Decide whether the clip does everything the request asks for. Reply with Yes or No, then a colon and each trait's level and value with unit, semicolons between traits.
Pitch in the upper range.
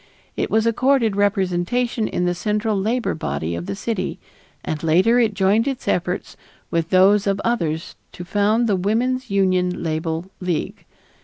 Yes: high, 195 Hz